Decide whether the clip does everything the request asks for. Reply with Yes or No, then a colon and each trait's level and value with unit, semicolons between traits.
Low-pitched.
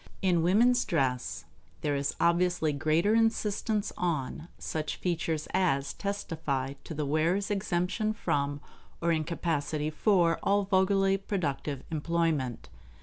No: medium, 170 Hz